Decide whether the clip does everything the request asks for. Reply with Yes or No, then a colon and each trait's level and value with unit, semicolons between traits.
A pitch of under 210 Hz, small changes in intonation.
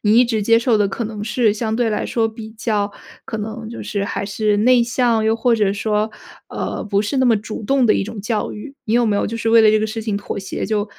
No: high, 220 Hz; narrow, 1.7 semitones